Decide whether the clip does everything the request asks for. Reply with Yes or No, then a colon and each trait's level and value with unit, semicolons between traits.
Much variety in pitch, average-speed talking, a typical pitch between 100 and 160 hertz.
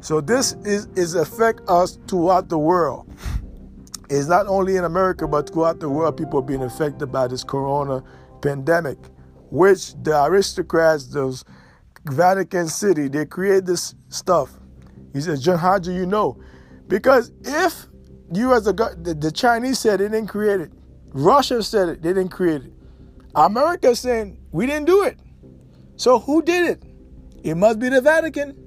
No: wide, 6.8 semitones; average, 165 wpm; medium, 175 Hz